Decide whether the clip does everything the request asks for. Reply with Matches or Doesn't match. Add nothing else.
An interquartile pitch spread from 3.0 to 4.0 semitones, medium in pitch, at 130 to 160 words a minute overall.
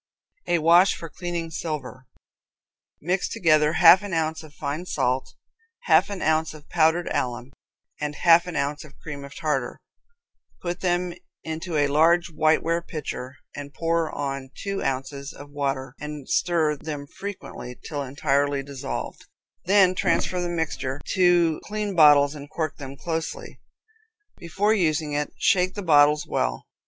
Matches